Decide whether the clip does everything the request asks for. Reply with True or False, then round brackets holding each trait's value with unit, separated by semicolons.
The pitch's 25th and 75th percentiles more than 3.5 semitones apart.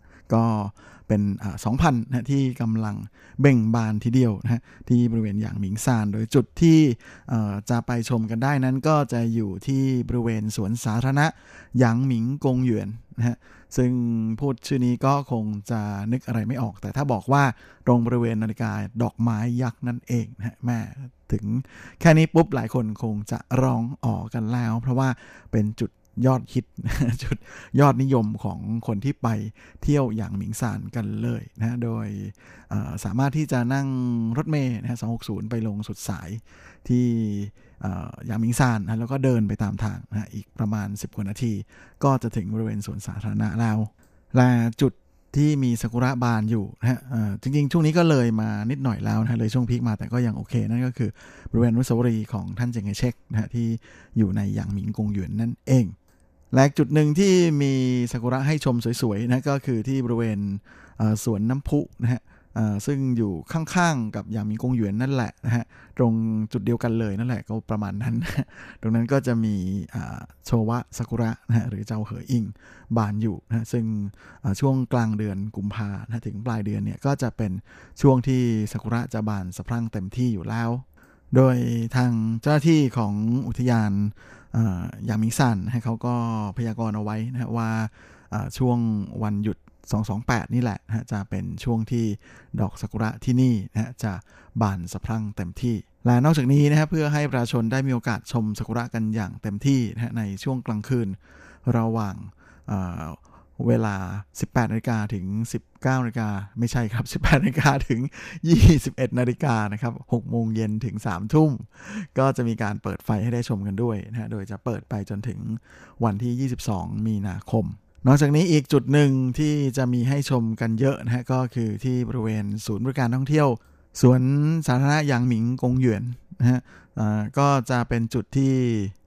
False (2.8 semitones)